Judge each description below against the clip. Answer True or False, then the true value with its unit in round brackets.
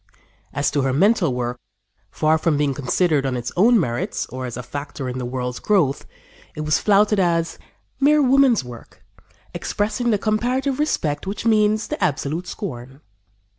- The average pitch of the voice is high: False (160 Hz)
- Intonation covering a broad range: True (8.3 semitones)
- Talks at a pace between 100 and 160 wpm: False (170 wpm)